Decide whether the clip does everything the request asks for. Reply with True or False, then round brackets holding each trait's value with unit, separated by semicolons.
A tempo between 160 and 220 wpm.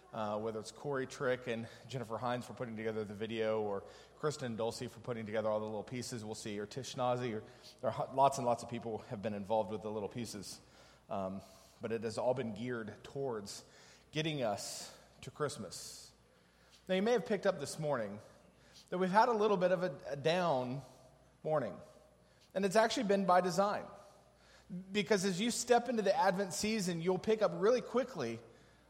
True (190 wpm)